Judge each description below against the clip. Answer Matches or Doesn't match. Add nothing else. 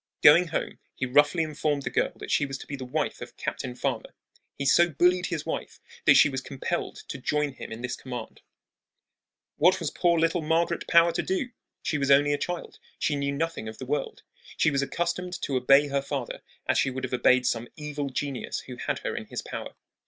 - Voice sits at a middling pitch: Matches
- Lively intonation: Doesn't match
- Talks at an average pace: Doesn't match